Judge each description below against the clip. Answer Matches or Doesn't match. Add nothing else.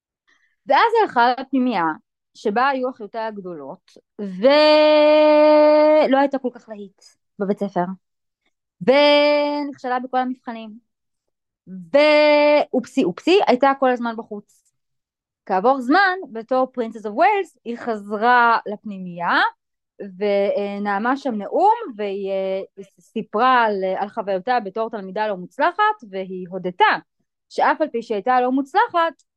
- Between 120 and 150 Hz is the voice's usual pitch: Doesn't match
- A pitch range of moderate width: Doesn't match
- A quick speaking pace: Doesn't match